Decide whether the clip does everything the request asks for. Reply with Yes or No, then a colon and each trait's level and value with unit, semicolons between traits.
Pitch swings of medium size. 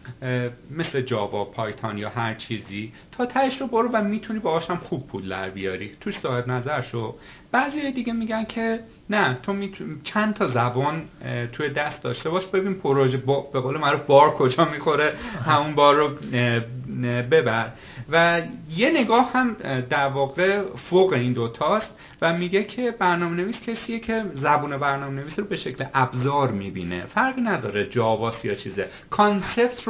No: wide, 8.5 semitones